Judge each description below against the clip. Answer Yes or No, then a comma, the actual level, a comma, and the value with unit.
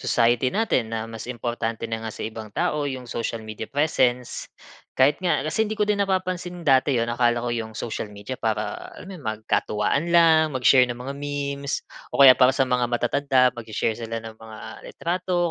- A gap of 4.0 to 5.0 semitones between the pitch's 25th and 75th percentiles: Yes, average, 4.3 semitones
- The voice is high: No, low, 125 Hz